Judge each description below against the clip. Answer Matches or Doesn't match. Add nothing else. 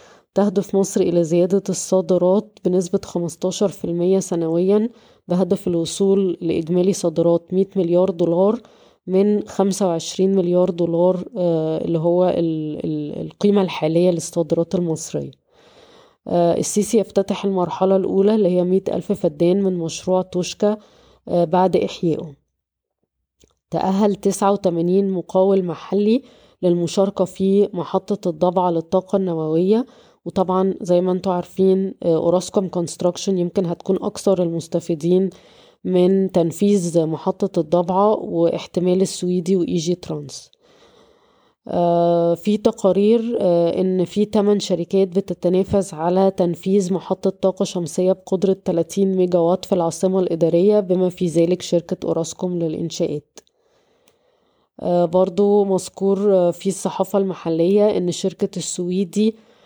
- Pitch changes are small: Matches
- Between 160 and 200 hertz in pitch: Matches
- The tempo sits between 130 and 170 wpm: Doesn't match